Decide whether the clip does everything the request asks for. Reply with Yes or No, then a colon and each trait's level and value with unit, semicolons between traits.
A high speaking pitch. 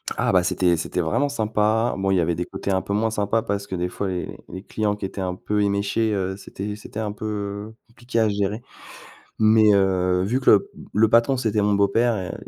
No: low, 105 Hz